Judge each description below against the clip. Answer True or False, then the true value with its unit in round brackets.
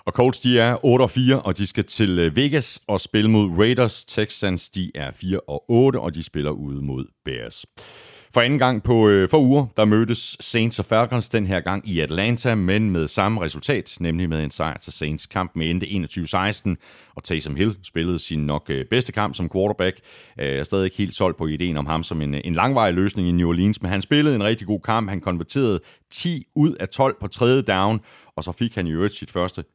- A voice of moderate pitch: False (100 Hz)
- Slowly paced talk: False (220 wpm)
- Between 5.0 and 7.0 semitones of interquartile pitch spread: True (5.3 semitones)